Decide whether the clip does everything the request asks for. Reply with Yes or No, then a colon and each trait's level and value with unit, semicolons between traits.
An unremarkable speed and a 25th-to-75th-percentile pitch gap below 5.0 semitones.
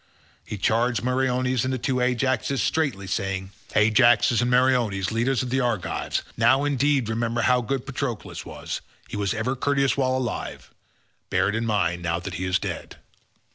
Yes: average, 170 wpm; average, 3.4 semitones